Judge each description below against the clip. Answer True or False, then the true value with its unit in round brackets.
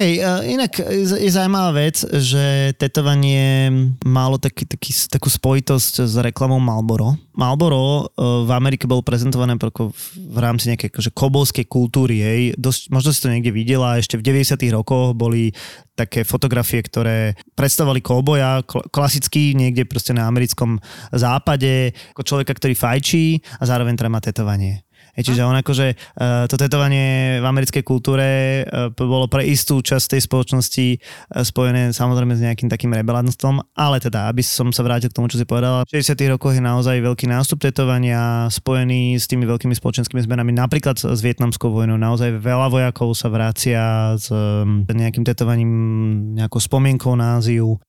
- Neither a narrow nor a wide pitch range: False (2.3 semitones)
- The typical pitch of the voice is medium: False (125 Hz)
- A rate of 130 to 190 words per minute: True (150 wpm)